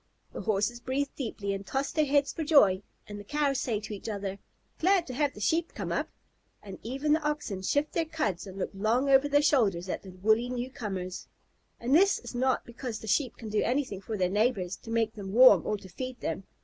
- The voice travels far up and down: Yes, wide, 5.8 semitones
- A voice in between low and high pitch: No, high, 235 Hz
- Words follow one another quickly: Yes, fast, 220 wpm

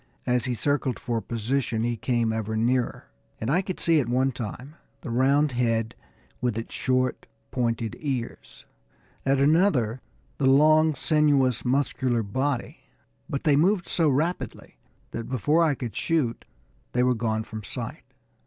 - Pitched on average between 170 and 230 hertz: No, low, 130 Hz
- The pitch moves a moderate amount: Yes, average, 3.7 semitones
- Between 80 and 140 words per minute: No, average, 150 wpm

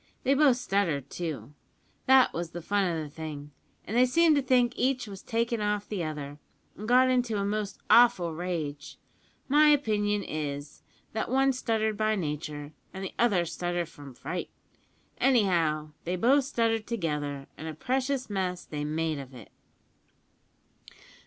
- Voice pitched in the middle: No, high, 195 Hz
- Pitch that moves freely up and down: Yes, wide, 7.6 semitones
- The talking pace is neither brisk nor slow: Yes, average, 160 wpm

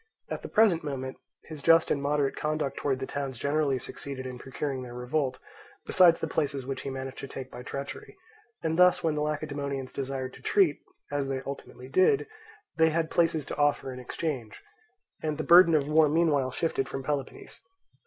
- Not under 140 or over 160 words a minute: No, average, 185 wpm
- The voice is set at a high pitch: No, medium, 140 Hz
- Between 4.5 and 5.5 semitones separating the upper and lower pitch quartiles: No, average, 2.8 semitones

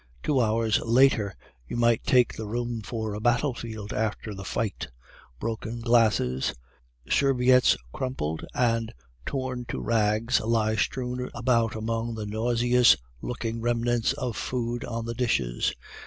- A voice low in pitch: Yes, low, 115 Hz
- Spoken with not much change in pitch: Yes, narrow, 1.8 semitones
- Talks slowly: Yes, slow, 130 wpm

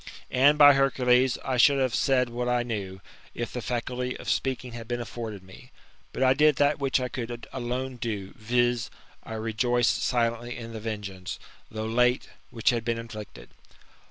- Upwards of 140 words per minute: Yes, average, 180 wpm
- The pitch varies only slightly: Yes, narrow, 2.1 semitones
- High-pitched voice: No, low, 120 Hz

